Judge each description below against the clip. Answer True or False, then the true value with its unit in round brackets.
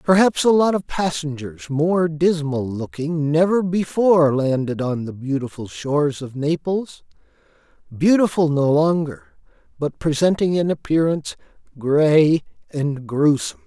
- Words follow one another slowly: True (115 wpm)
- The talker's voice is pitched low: False (155 Hz)